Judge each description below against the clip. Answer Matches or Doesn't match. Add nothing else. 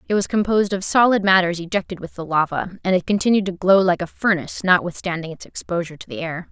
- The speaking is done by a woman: Matches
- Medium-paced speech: Doesn't match